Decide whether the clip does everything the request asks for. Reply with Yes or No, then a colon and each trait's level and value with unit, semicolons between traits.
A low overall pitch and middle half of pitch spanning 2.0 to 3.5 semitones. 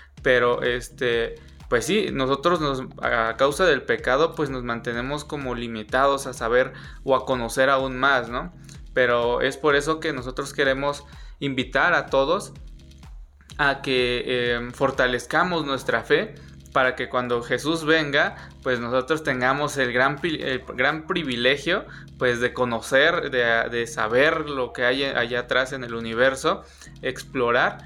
Yes: low, 130 Hz; narrow, 2.5 semitones